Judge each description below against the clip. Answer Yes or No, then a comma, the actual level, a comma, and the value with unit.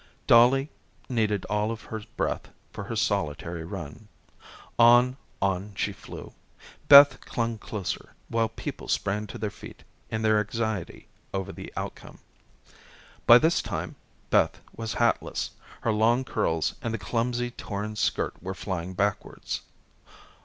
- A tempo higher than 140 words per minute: No, slow, 135 wpm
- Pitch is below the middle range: Yes, low, 110 Hz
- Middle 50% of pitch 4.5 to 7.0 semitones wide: No, average, 3.1 semitones